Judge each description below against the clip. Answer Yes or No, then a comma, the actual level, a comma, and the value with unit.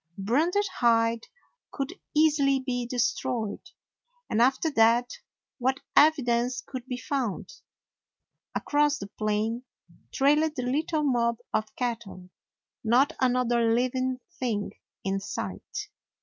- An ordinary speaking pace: No, slow, 115 wpm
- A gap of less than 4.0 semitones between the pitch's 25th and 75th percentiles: Yes, average, 3.3 semitones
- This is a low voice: No, very high, 250 Hz